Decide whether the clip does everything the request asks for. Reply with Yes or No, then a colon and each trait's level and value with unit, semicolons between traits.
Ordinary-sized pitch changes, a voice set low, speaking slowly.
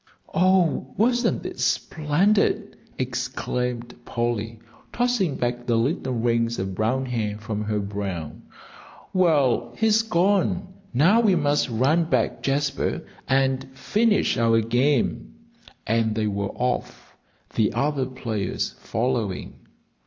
No: wide, 6.4 semitones; low, 125 Hz; slow, 115 wpm